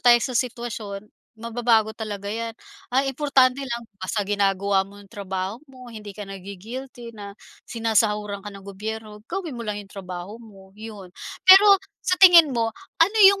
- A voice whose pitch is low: No, high, 220 Hz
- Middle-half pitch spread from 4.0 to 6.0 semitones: No, average, 3.4 semitones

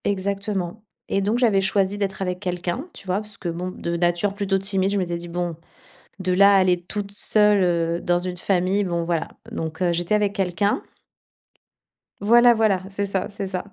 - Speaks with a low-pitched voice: No, high, 190 Hz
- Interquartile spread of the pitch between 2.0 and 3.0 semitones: Yes, narrow, 2.4 semitones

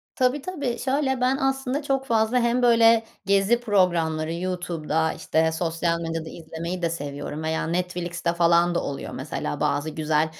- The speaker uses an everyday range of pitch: No, wide, 6.8 semitones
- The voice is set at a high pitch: No, medium, 175 Hz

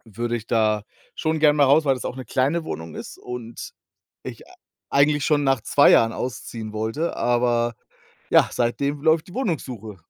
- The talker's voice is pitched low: Yes, low, 130 Hz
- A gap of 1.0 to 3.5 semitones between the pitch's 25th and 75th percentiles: No, average, 4.1 semitones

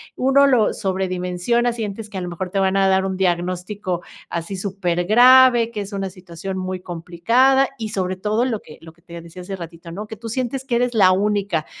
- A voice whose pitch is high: Yes, high, 195 Hz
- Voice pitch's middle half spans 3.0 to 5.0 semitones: Yes, average, 4.0 semitones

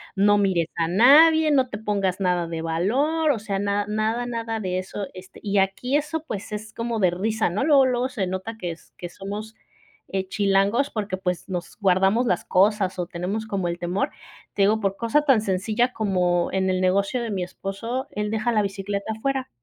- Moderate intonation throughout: Yes, average, 3.5 semitones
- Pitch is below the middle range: No, high, 205 Hz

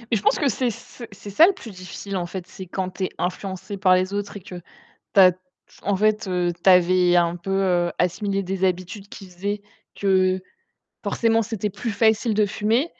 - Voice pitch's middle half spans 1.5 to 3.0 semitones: Yes, narrow, 2.5 semitones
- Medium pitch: No, high, 195 Hz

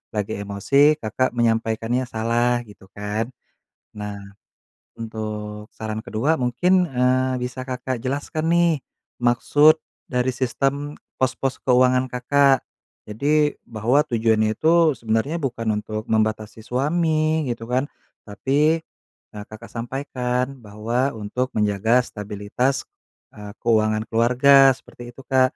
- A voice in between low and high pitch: No, low, 125 Hz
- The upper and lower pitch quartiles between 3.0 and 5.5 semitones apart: Yes, average, 3.8 semitones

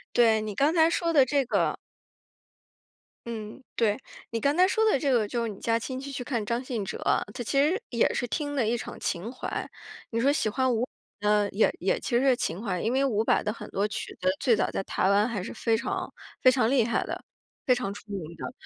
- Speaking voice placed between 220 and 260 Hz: Yes, high, 235 Hz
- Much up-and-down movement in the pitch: No, average, 4.0 semitones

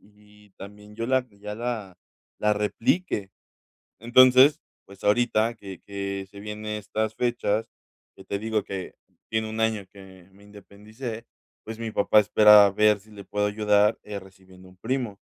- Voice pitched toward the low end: Yes, low, 105 Hz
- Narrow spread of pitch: Yes, narrow, 1.8 semitones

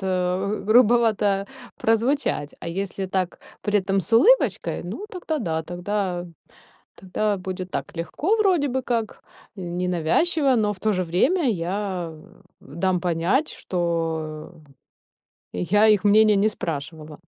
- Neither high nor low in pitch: No, high, 195 Hz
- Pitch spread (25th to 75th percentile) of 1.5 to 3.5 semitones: No, average, 4.1 semitones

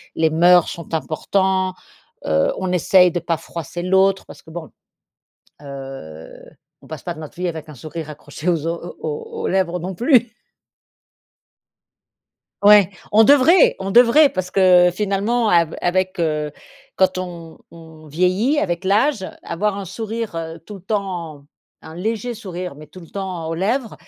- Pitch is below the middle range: No, medium, 180 Hz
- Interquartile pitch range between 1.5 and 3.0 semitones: No, average, 3.4 semitones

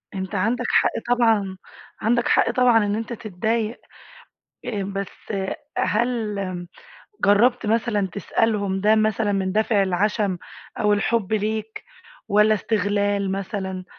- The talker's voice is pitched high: Yes, high, 210 Hz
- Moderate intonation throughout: No, narrow, 2.2 semitones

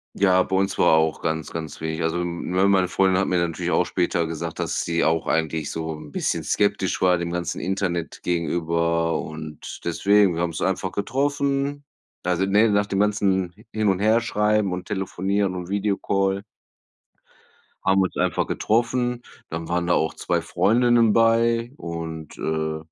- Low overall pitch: Yes, very low, 95 Hz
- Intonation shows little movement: No, average, 3.6 semitones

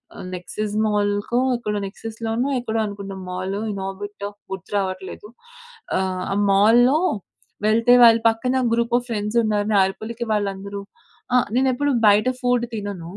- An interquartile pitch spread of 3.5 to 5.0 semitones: No, average, 2.8 semitones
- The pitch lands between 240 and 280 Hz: No, high, 210 Hz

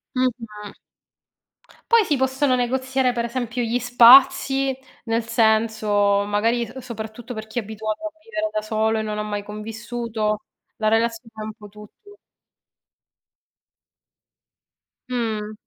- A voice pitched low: No, high, 230 Hz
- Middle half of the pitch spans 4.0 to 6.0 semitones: No, narrow, 2.6 semitones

